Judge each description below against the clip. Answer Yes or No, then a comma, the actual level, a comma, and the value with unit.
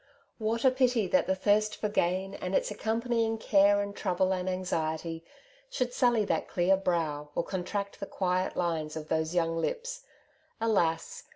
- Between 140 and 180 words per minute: Yes, average, 170 wpm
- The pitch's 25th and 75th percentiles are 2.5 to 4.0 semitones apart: No, average, 4.4 semitones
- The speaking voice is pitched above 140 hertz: Yes, high, 190 Hz